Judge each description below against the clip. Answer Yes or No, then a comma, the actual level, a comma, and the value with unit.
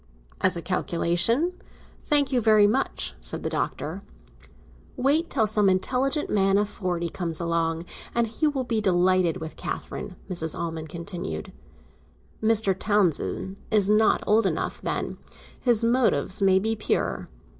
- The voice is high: Yes, high, 195 Hz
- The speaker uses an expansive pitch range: No, average, 4.6 semitones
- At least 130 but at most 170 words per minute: Yes, average, 140 wpm